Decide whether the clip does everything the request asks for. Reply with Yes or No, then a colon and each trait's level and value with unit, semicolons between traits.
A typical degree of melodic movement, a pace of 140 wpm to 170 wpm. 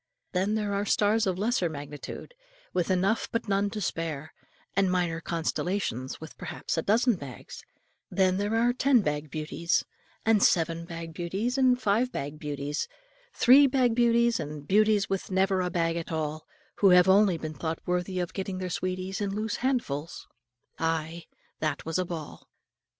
Yes: average, 4.4 semitones; average, 165 wpm